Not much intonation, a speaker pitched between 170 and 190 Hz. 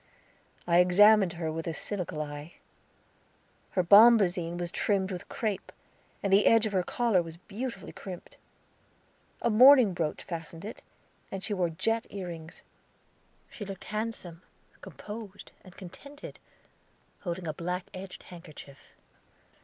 No: average, 3.7 semitones; medium, 185 Hz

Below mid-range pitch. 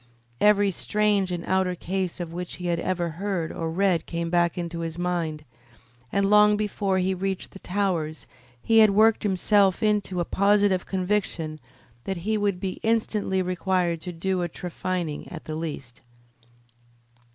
No: medium, 185 Hz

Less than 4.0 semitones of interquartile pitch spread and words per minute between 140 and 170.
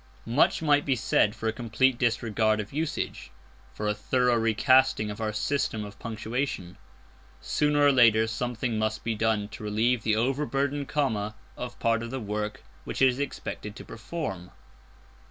Yes: average, 3.5 semitones; average, 165 wpm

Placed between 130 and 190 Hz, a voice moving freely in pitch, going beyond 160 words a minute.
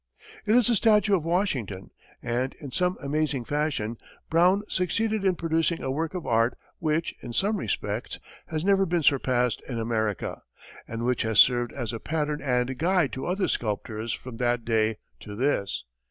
Yes: medium, 140 Hz; wide, 7.0 semitones; average, 170 wpm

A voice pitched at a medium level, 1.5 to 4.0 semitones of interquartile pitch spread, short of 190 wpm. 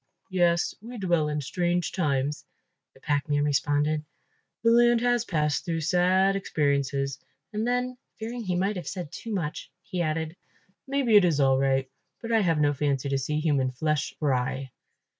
No: medium, 160 Hz; wide, 5.4 semitones; average, 165 wpm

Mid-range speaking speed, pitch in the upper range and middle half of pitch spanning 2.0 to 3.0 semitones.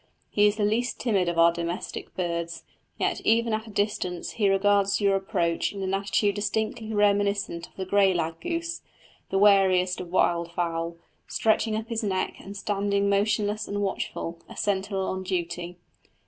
Yes: average, 170 wpm; high, 200 Hz; average, 2.7 semitones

